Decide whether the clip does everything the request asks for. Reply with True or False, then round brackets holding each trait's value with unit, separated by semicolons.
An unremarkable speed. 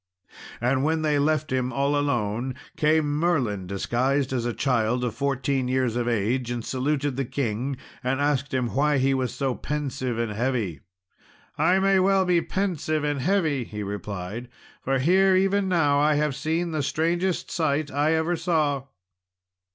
True (165 wpm)